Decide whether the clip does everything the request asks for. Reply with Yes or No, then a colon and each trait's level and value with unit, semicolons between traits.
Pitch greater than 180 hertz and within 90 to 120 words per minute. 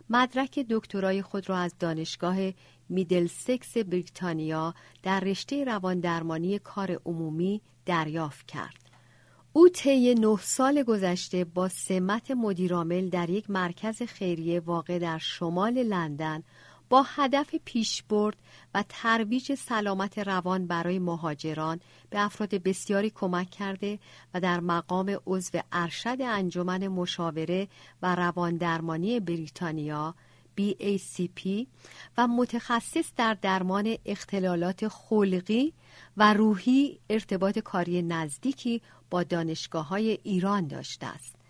Yes: high, 190 Hz; average, 110 wpm